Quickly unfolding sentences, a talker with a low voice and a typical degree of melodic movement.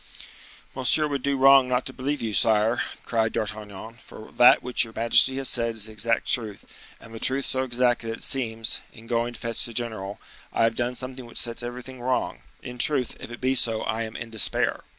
No: fast, 215 wpm; low, 120 Hz; narrow, 2.2 semitones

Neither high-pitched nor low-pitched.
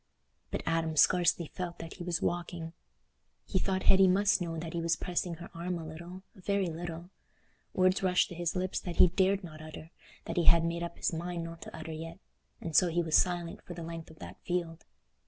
Yes: medium, 170 Hz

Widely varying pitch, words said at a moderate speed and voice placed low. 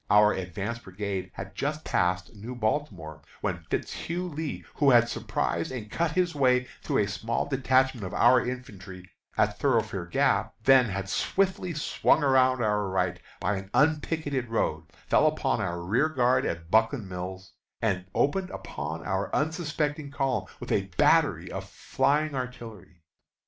Yes: wide, 6.8 semitones; average, 150 wpm; low, 115 Hz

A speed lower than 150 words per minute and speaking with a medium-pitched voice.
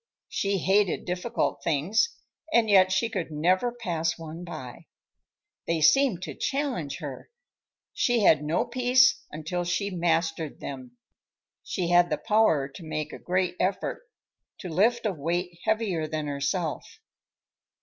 Yes: average, 140 wpm; medium, 175 Hz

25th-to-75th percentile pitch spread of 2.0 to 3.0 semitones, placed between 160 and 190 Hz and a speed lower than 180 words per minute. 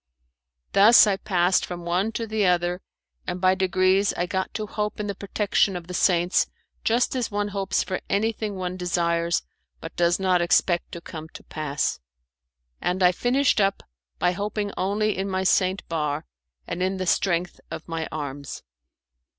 Yes: narrow, 2.6 semitones; medium, 185 Hz; average, 170 wpm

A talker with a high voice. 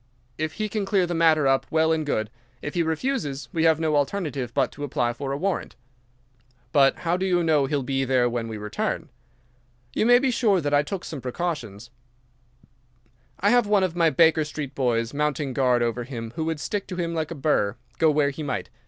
No: medium, 150 Hz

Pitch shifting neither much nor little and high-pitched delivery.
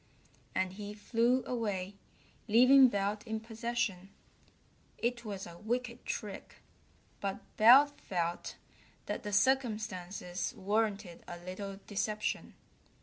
Yes: average, 3.5 semitones; high, 210 Hz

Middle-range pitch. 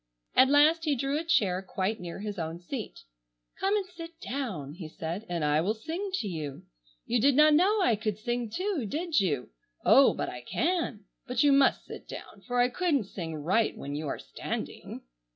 No: high, 235 Hz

